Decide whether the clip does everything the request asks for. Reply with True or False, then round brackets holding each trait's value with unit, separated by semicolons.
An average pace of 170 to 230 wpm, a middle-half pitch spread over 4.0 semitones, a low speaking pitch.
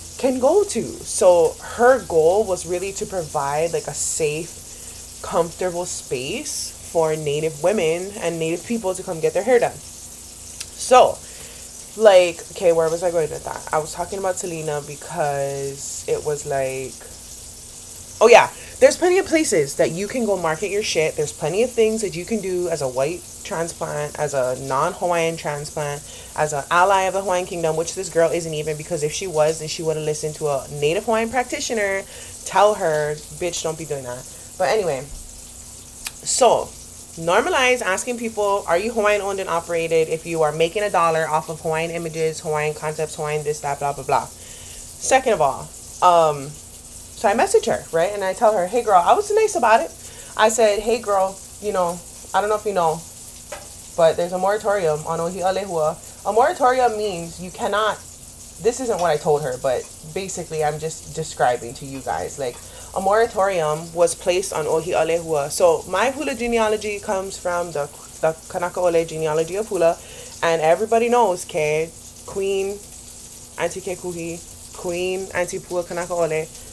False (180 wpm; 4.8 semitones; 170 Hz)